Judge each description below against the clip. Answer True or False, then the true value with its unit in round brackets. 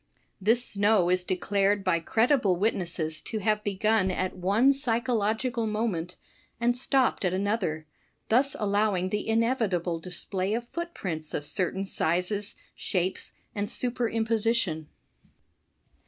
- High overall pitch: True (205 Hz)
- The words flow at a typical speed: False (120 wpm)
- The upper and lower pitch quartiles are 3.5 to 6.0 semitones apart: True (3.8 semitones)